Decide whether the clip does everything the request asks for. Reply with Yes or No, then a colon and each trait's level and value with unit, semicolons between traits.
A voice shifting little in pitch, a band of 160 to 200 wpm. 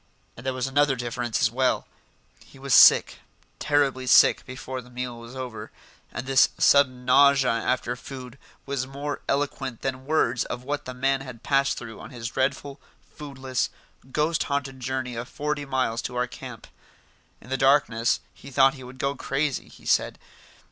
Yes: narrow, 1.7 semitones; average, 170 wpm